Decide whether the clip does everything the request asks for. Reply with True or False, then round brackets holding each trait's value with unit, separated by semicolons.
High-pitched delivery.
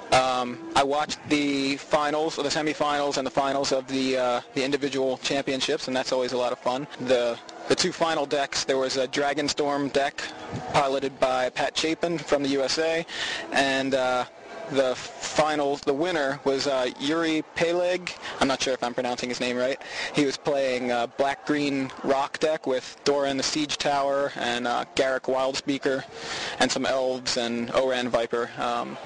False (135 Hz)